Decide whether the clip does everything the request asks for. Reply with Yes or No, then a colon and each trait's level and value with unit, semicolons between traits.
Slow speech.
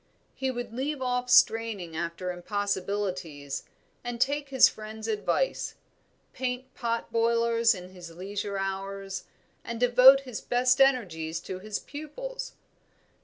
Yes: slow, 120 wpm